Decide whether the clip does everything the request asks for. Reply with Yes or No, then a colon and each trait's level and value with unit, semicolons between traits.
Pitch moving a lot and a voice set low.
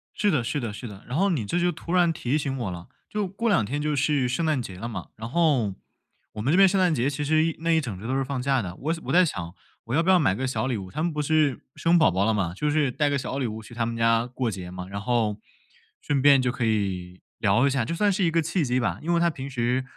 Yes: wide, 6.1 semitones; low, 130 Hz